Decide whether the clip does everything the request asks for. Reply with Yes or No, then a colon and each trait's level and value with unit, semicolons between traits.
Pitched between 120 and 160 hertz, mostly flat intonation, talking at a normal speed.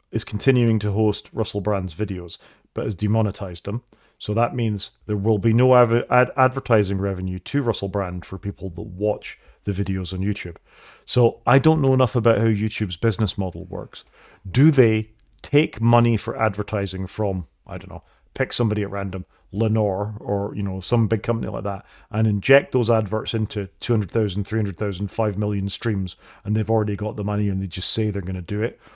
No: low, 105 Hz; narrow, 2.3 semitones; average, 190 wpm